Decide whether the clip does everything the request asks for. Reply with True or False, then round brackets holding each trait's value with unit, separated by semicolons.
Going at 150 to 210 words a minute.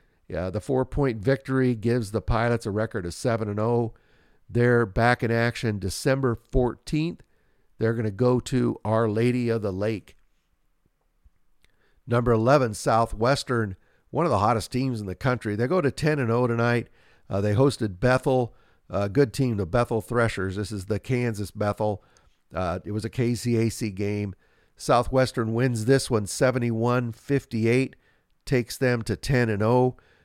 True (160 wpm)